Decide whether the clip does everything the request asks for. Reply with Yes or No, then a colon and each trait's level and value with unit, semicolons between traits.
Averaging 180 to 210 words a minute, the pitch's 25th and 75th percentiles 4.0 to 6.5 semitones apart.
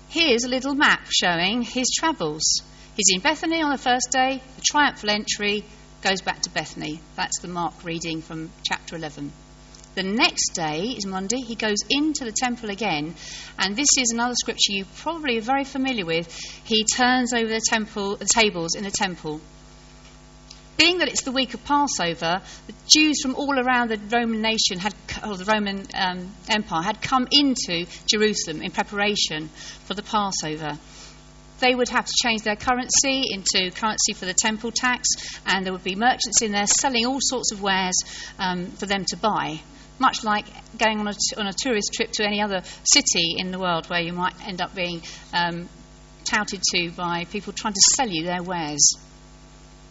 Yes: average, 185 wpm; wide, 5.6 semitones